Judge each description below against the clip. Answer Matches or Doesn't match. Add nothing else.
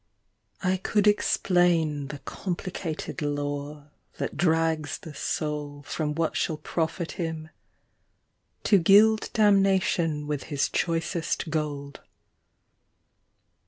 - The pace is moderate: Doesn't match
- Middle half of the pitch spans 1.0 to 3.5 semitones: Matches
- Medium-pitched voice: Matches